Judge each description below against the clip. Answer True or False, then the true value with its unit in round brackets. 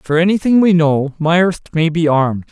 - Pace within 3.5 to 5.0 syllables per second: True (4.7 syllables/s)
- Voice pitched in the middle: True (165 Hz)